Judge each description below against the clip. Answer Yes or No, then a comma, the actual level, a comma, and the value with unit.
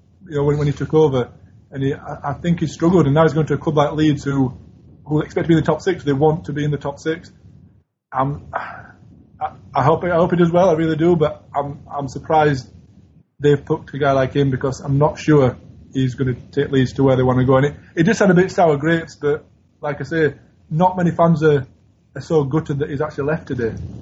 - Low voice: No, medium, 145 Hz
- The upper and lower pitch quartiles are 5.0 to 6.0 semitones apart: No, average, 2.8 semitones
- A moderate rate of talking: No, fast, 245 wpm